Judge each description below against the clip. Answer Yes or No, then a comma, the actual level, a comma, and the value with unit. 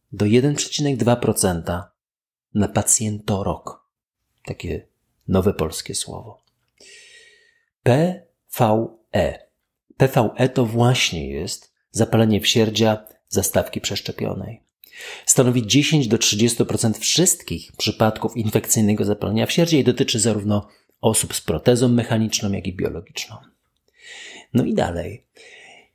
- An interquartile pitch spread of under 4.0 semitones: No, average, 5.1 semitones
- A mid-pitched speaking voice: No, low, 115 Hz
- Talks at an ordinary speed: No, slow, 90 wpm